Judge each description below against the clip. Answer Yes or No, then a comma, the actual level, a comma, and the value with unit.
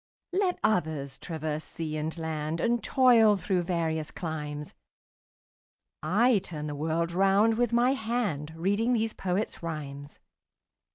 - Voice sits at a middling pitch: Yes, medium, 170 Hz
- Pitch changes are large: Yes, wide, 6.2 semitones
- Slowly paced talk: Yes, slow, 130 wpm